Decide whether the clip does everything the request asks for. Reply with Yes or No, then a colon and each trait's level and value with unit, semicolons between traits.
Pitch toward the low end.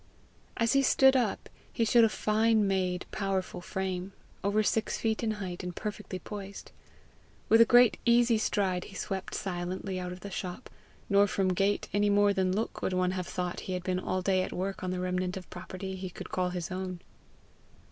No: high, 190 Hz